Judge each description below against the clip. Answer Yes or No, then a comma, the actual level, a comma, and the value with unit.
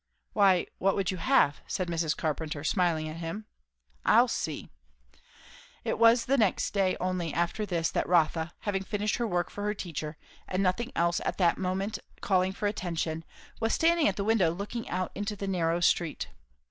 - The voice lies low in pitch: No, medium, 185 Hz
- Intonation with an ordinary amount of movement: Yes, average, 3.5 semitones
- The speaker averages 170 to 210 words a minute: Yes, average, 180 wpm